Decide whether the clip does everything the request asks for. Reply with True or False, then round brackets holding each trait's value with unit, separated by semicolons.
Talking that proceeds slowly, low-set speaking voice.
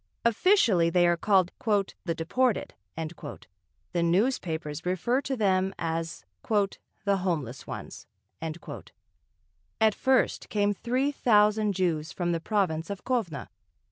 False (110 wpm; 185 Hz)